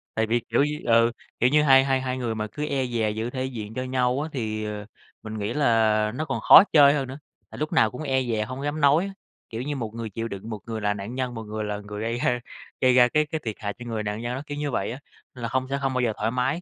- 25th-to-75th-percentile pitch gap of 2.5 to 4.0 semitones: Yes, average, 3.5 semitones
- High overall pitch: No, low, 120 Hz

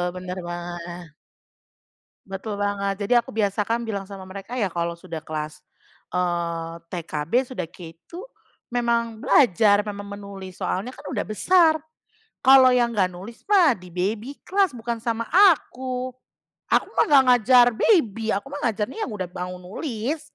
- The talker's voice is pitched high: Yes, high, 205 Hz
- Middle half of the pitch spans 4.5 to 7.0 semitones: Yes, average, 5.2 semitones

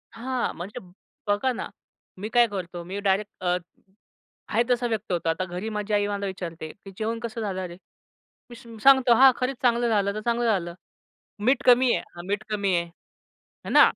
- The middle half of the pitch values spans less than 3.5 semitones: No, average, 4.3 semitones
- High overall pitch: Yes, high, 210 Hz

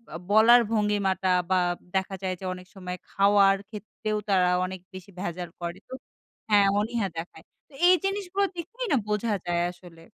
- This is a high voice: Yes, high, 195 Hz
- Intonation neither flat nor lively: Yes, average, 3.1 semitones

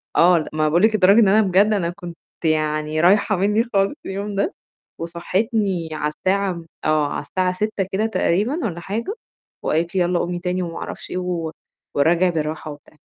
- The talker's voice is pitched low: No, medium, 180 Hz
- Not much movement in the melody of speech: No, average, 3.3 semitones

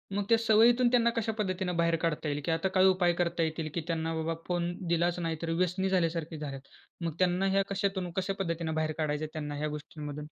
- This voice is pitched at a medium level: Yes, medium, 170 Hz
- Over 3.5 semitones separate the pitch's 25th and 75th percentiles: No, average, 3.0 semitones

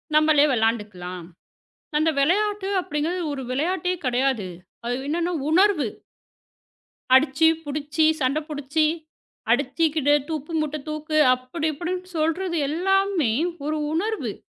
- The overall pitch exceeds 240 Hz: Yes, very high, 310 Hz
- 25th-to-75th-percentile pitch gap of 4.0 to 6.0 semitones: Yes, average, 4.3 semitones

